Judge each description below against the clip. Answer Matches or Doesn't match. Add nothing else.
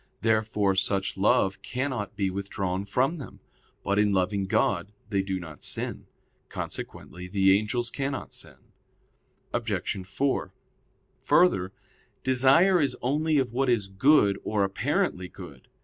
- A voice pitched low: Matches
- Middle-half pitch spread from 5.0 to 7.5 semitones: Matches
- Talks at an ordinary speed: Doesn't match